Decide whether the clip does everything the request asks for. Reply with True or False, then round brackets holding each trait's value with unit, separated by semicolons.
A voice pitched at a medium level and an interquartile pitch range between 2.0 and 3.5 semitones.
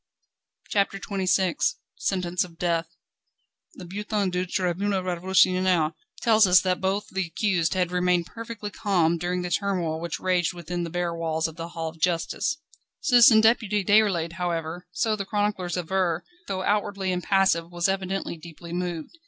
True (180 Hz; 2.5 semitones)